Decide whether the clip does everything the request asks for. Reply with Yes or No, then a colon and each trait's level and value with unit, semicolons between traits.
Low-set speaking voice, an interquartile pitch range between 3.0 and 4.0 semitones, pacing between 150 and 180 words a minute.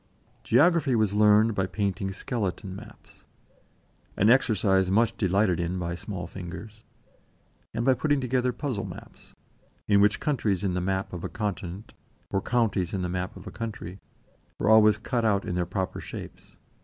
Yes: low, 100 Hz; average, 3.4 semitones; average, 165 wpm